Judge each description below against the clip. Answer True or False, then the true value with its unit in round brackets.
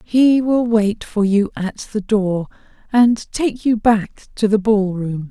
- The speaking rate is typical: True (180 wpm)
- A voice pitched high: True (215 Hz)